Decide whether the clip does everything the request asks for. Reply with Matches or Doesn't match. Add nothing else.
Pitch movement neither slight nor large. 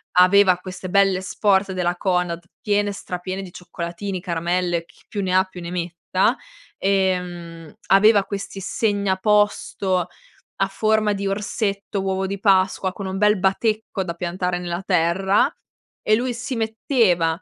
Doesn't match